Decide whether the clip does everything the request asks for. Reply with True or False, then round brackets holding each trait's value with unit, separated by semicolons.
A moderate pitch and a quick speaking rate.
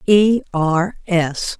False (180 Hz; 115 wpm)